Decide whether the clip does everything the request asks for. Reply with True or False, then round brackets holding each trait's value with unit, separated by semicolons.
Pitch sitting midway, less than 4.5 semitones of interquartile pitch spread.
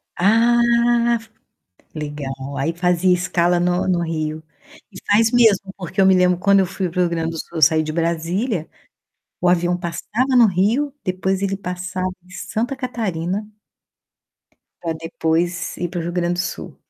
True (180 Hz; 2.7 semitones)